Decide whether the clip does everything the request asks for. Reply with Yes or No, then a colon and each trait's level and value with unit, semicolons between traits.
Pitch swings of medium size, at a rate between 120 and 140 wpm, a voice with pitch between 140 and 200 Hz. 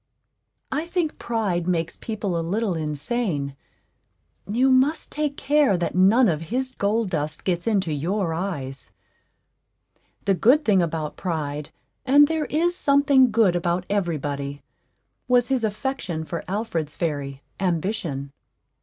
No: wide, 7.4 semitones; slow, 135 wpm; high, 190 Hz